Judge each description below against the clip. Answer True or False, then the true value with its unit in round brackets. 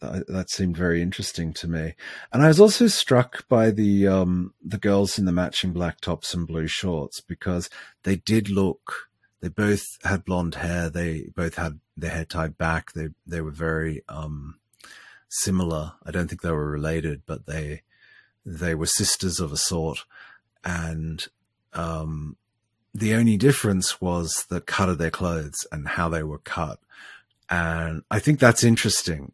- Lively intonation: False (3.4 semitones)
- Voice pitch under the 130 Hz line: True (85 Hz)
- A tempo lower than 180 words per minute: True (165 wpm)